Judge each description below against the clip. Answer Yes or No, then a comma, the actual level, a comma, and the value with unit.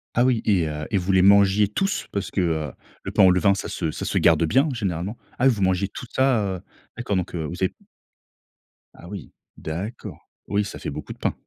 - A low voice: Yes, very low, 95 Hz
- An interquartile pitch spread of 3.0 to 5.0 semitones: Yes, average, 3.3 semitones